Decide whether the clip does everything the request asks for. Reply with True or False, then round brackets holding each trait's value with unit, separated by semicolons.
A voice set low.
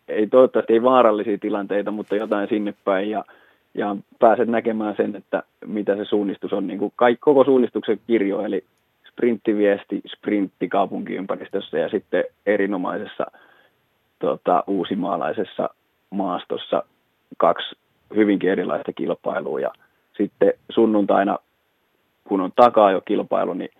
True (110 Hz)